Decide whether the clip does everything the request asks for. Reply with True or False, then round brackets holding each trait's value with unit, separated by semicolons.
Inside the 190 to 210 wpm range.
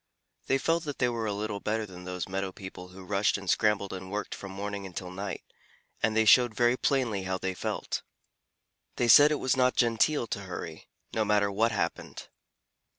True (195 wpm)